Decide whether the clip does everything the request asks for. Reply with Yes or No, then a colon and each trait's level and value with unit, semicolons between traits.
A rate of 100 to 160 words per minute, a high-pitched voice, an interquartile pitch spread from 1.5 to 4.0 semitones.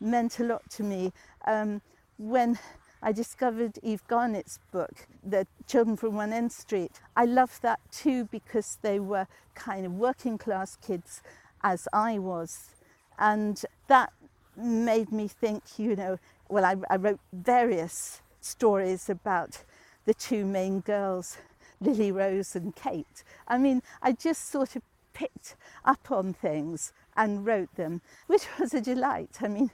Yes: average, 150 wpm; high, 220 Hz; average, 3.6 semitones